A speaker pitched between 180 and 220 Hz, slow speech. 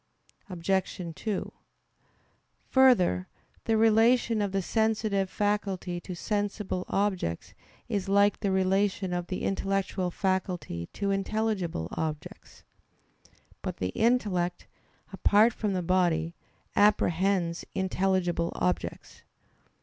Yes: high, 190 Hz; slow, 100 wpm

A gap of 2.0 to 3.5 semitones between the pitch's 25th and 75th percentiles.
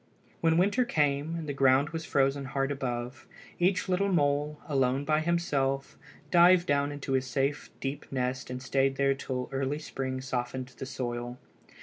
Yes: average, 2.7 semitones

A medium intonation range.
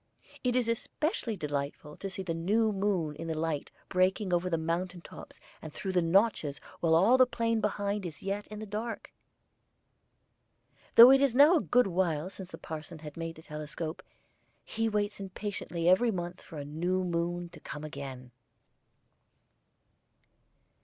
Yes: average, 4.4 semitones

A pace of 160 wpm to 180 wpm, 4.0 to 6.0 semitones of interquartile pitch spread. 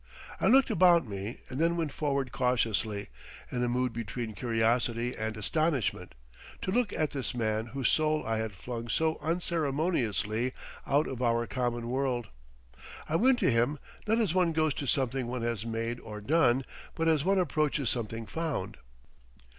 Yes: average, 165 wpm; wide, 5.4 semitones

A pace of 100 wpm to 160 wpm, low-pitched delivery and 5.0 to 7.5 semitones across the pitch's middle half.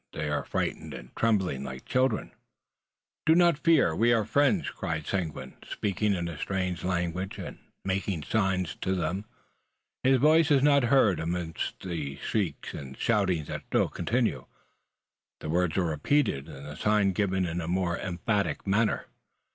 Yes: average, 155 wpm; very low, 95 Hz; wide, 5.4 semitones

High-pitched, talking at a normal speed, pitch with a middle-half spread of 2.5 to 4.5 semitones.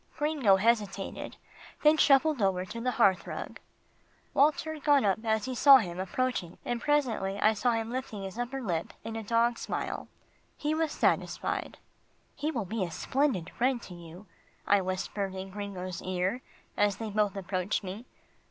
No: high, 220 Hz; average, 170 wpm; average, 5.1 semitones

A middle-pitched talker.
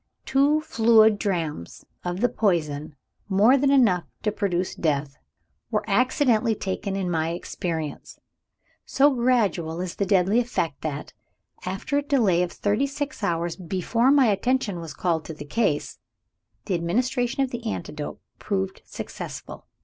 No: high, 195 Hz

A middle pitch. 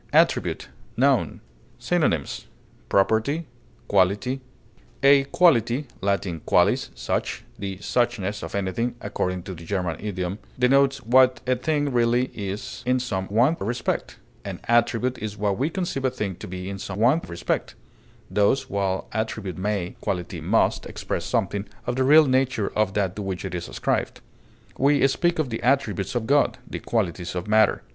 No: low, 110 Hz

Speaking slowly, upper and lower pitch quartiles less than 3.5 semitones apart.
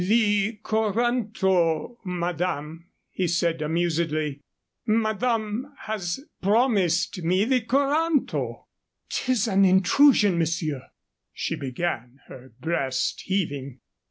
No: slow, 90 wpm; average, 5.2 semitones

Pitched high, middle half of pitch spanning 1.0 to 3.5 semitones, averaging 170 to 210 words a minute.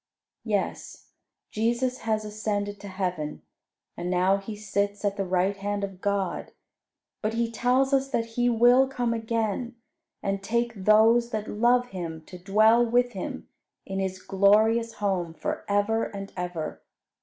No: high, 210 Hz; average, 3.0 semitones; average, 150 wpm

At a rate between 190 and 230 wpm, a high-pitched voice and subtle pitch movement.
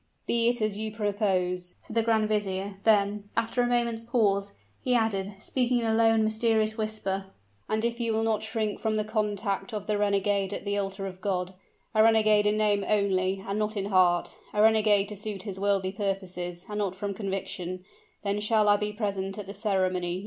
Yes: average, 200 wpm; high, 210 Hz; narrow, 2.0 semitones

